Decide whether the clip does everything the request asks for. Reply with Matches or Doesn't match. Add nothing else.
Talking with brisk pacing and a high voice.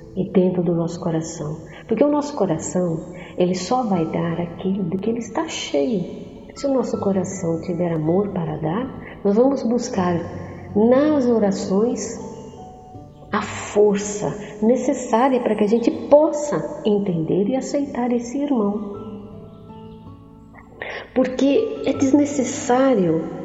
Doesn't match